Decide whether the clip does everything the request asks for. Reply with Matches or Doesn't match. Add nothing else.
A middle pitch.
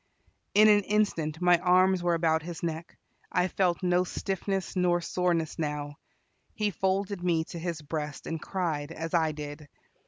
Matches